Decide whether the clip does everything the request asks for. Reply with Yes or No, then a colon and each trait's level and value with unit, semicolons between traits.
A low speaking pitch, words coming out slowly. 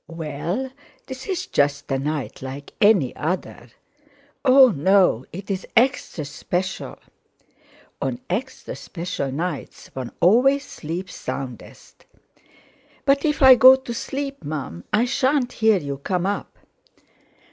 No: medium, 185 Hz; slow, 115 wpm